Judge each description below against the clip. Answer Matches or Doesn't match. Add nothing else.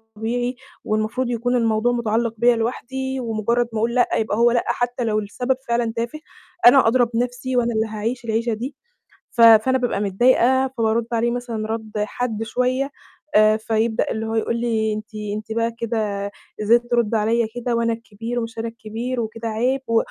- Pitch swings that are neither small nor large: Doesn't match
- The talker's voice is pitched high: Matches